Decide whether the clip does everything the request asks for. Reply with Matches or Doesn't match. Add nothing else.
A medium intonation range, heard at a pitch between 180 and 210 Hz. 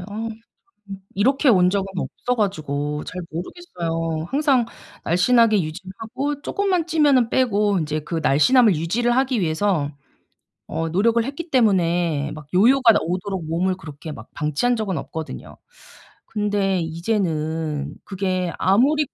Doesn't match